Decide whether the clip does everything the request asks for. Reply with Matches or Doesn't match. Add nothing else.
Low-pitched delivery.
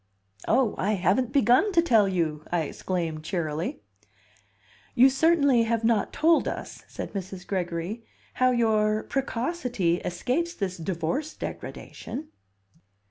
Doesn't match